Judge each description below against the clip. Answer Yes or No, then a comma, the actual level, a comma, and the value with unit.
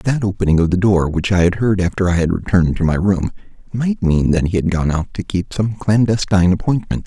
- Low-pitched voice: Yes, very low, 95 Hz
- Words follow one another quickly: Yes, fast, 240 wpm